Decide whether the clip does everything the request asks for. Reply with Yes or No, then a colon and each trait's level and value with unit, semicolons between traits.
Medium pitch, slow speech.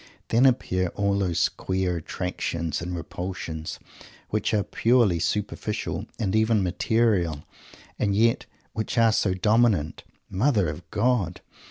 No: low, 100 Hz; slow, 125 wpm